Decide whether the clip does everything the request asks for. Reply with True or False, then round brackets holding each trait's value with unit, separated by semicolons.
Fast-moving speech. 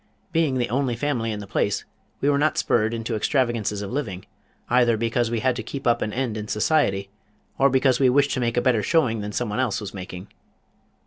True (215 wpm)